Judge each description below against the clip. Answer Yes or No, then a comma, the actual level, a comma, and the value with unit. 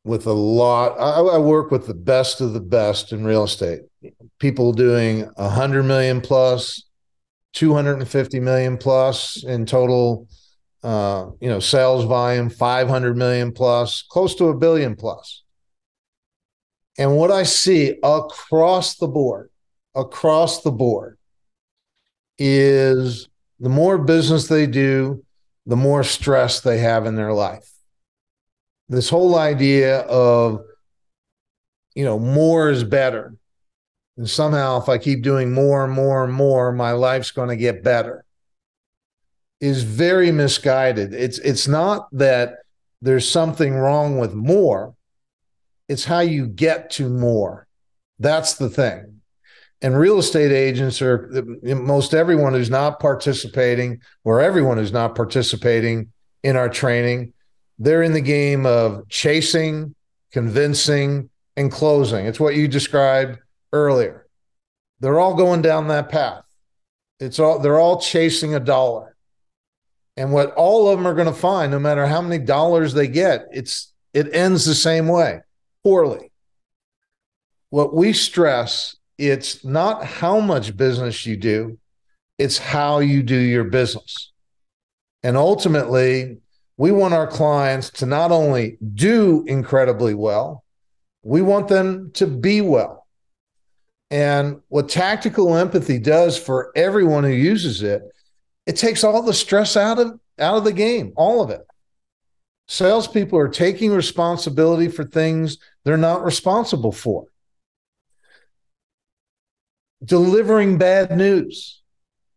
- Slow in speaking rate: Yes, slow, 130 wpm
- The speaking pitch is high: No, low, 135 Hz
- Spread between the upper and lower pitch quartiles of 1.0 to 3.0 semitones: No, average, 4.7 semitones